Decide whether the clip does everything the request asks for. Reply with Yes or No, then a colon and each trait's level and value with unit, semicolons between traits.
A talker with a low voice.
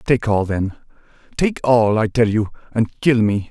Yes: low, 115 Hz